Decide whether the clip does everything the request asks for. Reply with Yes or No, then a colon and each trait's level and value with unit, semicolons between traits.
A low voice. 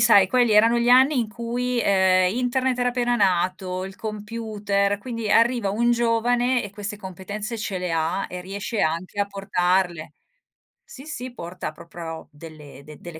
No: high, 205 Hz